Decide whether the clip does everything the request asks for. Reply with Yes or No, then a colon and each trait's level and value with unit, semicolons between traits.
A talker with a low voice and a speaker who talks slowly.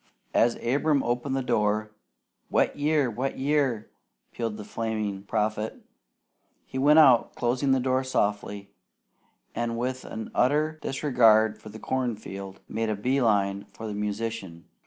No: low, 115 Hz; average, 145 wpm